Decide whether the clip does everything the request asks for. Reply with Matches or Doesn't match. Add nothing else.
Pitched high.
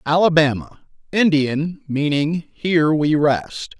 Doesn't match